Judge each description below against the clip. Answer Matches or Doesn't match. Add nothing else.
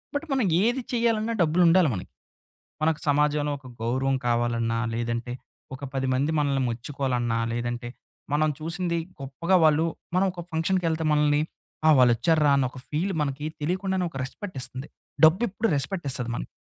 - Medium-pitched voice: Matches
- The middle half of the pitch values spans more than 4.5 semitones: Matches